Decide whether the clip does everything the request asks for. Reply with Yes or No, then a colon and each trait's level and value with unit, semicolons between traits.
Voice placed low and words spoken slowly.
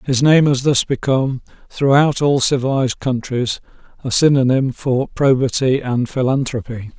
Yes: low, 130 Hz; slow, 130 wpm